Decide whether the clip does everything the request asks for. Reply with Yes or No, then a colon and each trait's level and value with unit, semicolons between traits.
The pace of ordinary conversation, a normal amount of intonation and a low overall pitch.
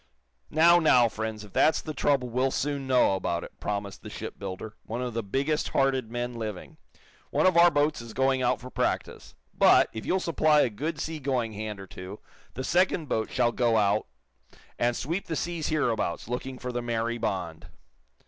Yes: average, 190 wpm; average, 4.9 semitones; low, 125 Hz